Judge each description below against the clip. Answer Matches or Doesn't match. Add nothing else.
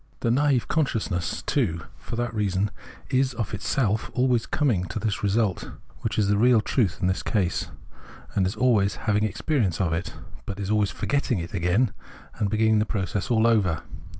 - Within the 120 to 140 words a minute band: Doesn't match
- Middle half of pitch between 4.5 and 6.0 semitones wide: Doesn't match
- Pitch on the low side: Matches